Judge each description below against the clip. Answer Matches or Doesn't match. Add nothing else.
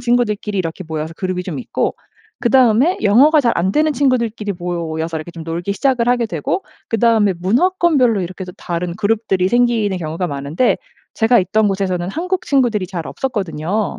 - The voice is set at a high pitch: Matches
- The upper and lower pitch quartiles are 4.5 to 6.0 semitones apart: Matches